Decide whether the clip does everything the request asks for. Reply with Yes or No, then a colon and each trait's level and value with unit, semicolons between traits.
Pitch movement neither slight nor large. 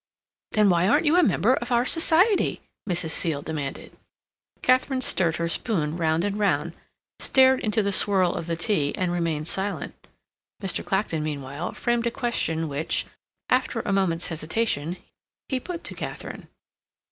No: wide, 6.5 semitones